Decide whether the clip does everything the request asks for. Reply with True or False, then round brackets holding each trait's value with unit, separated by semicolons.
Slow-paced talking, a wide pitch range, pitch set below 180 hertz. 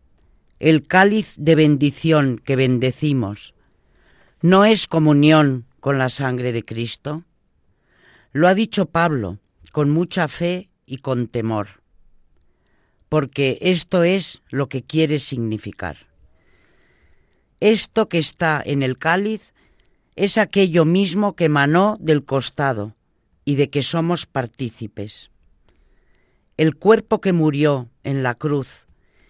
True (115 wpm; 8.0 semitones; 140 Hz)